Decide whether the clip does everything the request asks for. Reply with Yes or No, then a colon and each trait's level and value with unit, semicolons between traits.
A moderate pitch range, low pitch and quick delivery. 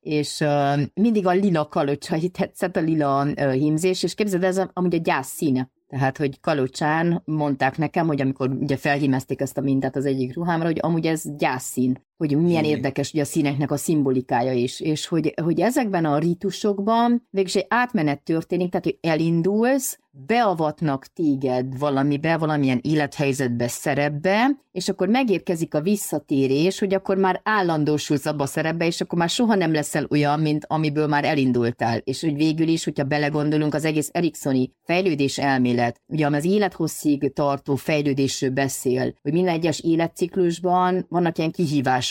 No: average, 4.1 semitones; medium, 155 Hz; fast, 160 wpm